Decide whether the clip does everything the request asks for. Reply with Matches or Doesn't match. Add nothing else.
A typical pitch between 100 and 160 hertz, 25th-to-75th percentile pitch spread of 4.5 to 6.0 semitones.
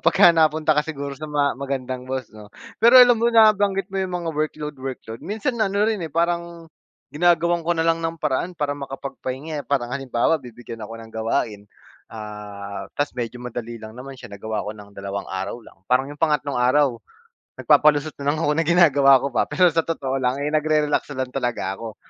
Matches